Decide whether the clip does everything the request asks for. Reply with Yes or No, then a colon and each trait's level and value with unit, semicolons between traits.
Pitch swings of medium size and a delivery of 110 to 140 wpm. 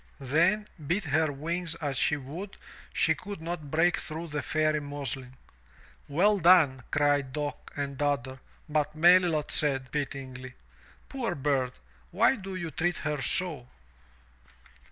Yes: average, 3.7 semitones; slow, 135 wpm